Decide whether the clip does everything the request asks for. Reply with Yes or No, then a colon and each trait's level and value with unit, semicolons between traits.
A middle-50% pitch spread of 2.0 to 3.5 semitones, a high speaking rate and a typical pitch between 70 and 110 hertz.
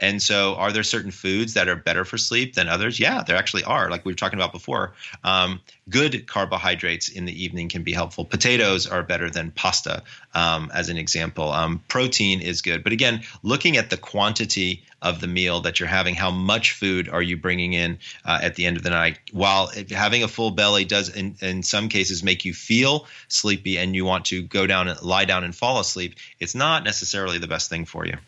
Yes: average, 2.7 semitones; fast, 225 wpm; very low, 95 Hz